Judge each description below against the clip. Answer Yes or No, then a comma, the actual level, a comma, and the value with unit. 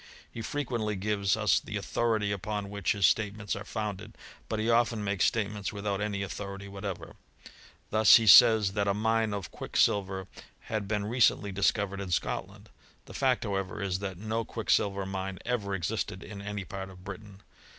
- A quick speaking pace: No, average, 170 wpm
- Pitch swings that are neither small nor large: No, narrow, 1.8 semitones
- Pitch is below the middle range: Yes, low, 100 Hz